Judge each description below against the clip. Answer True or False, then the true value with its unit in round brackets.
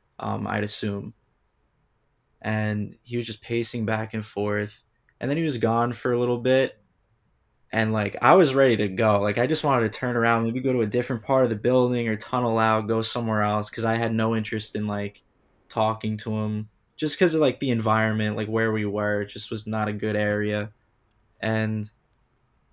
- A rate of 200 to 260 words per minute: True (205 wpm)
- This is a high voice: False (110 Hz)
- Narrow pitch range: True (2.2 semitones)